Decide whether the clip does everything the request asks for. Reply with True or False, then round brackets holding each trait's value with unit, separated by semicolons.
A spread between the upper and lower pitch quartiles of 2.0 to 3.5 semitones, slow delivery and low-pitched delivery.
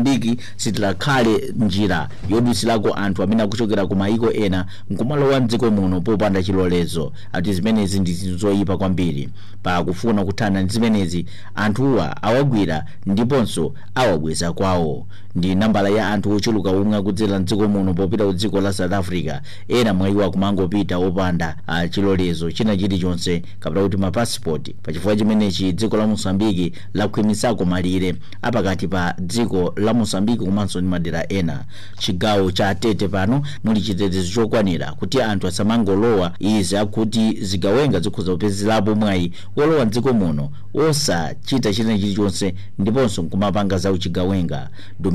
True (2.7 semitones; 95 wpm; 100 Hz)